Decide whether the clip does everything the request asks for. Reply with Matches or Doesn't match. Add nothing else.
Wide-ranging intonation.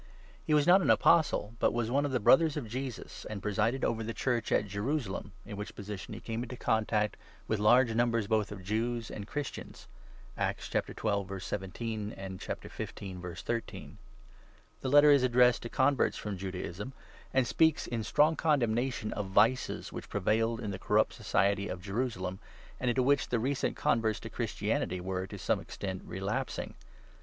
Doesn't match